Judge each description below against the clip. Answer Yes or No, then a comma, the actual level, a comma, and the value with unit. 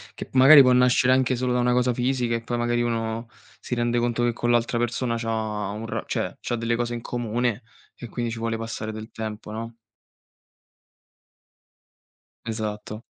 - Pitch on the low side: Yes, low, 120 Hz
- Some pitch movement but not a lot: No, narrow, 1.4 semitones